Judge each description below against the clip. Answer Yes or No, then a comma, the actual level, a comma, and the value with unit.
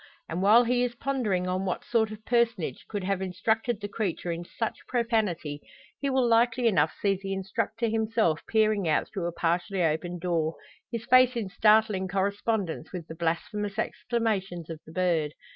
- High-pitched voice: Yes, high, 200 Hz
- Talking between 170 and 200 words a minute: Yes, average, 175 wpm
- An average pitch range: Yes, average, 4.5 semitones